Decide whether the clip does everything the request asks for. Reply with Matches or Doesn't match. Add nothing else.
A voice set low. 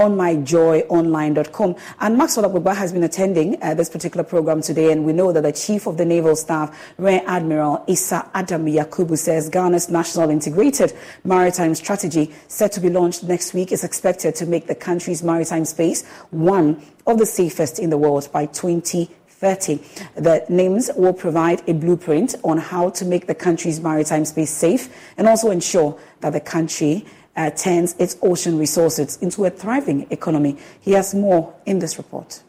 Doesn't match